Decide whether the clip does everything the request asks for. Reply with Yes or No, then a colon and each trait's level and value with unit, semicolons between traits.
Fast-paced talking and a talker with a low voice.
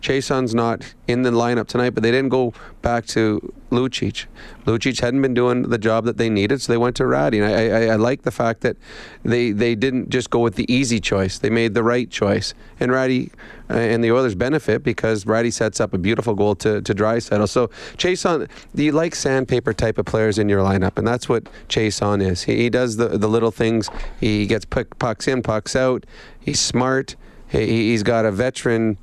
Yes: fast, 215 wpm; low, 115 Hz